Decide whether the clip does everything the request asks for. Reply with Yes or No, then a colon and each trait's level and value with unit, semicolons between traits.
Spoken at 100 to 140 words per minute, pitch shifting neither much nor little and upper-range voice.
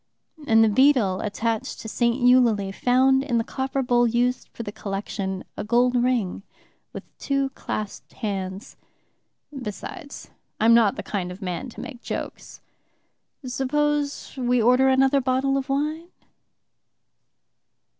Yes: slow, 135 wpm; average, 3.8 semitones; high, 245 Hz